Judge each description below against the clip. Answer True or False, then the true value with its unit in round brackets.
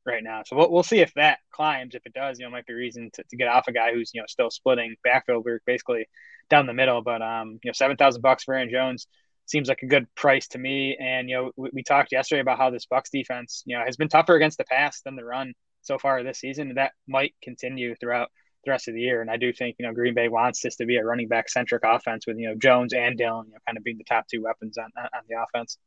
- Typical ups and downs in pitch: False (2.2 semitones)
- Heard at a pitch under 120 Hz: False (125 Hz)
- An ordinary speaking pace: False (280 wpm)